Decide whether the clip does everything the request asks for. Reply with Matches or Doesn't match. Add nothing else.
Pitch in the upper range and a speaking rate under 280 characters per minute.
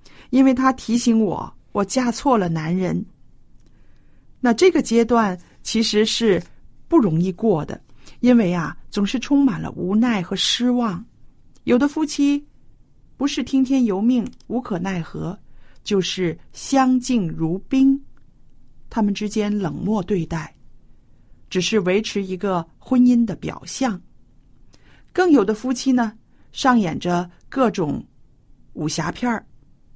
Matches